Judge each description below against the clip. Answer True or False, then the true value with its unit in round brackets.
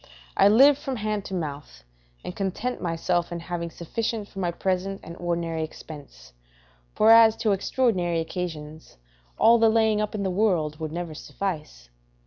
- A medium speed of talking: True (160 wpm)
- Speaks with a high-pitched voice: False (180 Hz)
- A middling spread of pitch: True (4.6 semitones)